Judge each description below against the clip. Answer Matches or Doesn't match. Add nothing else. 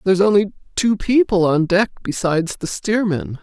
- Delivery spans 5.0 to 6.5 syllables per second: Matches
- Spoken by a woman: Matches